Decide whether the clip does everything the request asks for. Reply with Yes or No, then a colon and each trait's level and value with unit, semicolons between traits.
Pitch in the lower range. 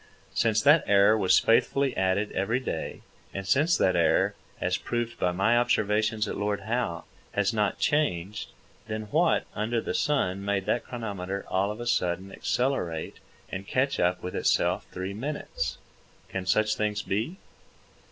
Yes: low, 105 Hz